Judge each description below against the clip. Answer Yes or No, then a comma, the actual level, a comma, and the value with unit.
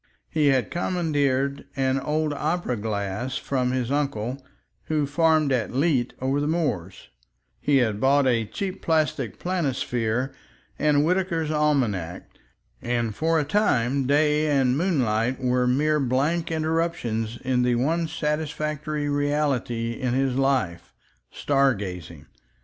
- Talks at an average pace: No, slow, 125 wpm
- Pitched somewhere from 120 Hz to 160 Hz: Yes, low, 135 Hz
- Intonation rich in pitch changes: No, average, 3.8 semitones